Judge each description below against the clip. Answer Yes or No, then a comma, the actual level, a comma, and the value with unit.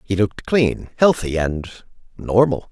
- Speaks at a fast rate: No, slow, 135 wpm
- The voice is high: No, low, 110 Hz